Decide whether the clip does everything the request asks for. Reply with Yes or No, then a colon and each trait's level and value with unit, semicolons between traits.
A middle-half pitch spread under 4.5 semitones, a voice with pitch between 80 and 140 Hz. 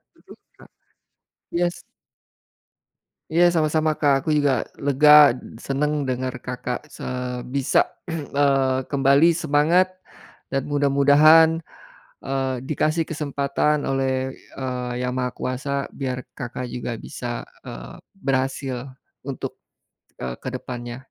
Yes: narrow, 2.5 semitones; low, 135 Hz